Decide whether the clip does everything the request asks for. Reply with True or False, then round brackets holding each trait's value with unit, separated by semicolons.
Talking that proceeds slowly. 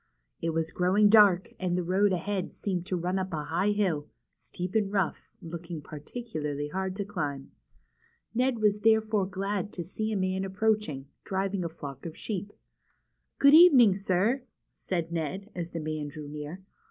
False (170 wpm)